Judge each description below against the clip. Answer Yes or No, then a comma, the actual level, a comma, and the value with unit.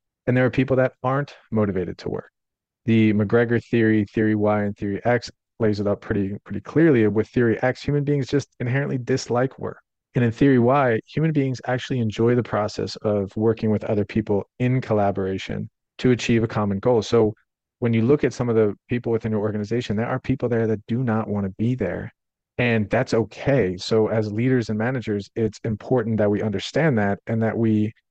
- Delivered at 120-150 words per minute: No, average, 200 wpm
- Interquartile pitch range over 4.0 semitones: No, average, 2.8 semitones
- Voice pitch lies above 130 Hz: No, low, 115 Hz